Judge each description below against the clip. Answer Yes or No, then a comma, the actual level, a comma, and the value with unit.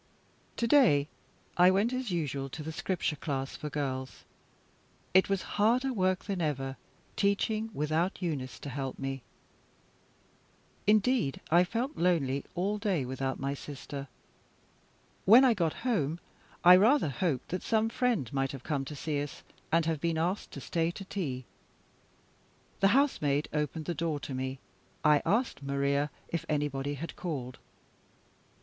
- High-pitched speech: No, medium, 160 Hz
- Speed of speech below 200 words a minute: Yes, average, 150 wpm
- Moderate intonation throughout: No, wide, 6.0 semitones